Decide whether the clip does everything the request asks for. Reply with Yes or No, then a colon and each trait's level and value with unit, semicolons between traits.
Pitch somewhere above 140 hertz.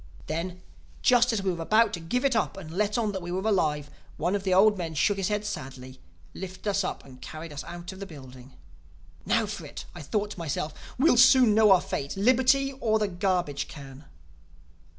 Yes: high, 190 Hz